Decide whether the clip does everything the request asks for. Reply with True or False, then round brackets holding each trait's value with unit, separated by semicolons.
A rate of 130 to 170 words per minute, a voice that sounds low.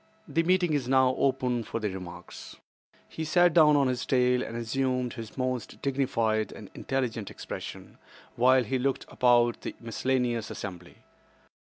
True (145 wpm; 125 Hz)